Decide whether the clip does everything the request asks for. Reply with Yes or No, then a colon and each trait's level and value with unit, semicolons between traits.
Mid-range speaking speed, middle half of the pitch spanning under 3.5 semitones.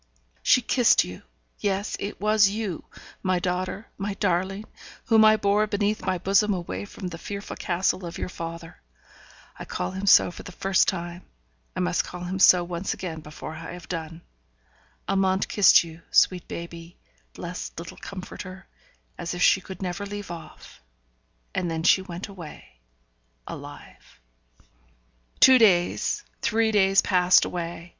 Yes: average, 150 wpm; average, 2.7 semitones